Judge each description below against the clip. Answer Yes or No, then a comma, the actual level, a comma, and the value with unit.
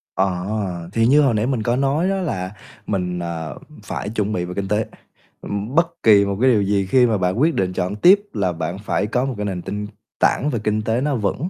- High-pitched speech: No, low, 105 Hz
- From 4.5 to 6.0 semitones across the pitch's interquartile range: Yes, average, 4.8 semitones